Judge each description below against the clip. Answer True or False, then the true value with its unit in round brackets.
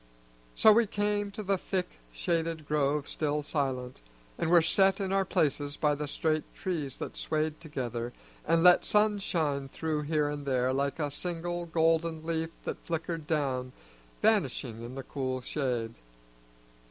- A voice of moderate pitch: True (155 Hz)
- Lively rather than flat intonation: False (3.5 semitones)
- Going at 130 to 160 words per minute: True (155 wpm)